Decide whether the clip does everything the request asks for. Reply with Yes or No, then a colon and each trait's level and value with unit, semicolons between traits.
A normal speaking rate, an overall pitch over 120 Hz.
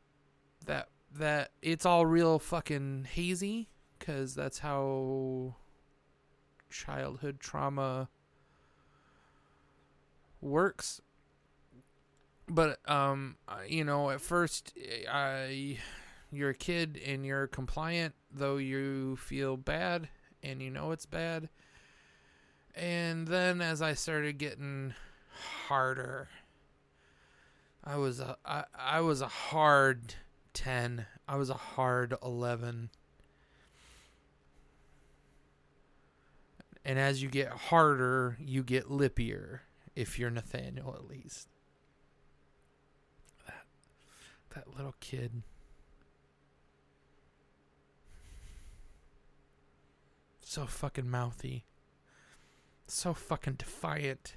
No: slow, 85 wpm; low, 135 Hz